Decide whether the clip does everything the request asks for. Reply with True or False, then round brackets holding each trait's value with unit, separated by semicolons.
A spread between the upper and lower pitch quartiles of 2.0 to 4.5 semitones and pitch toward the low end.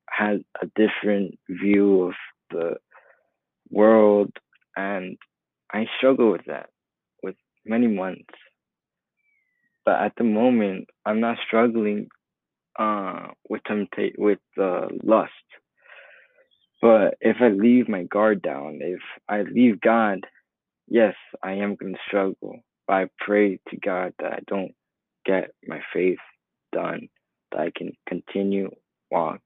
True (2.8 semitones; 105 Hz)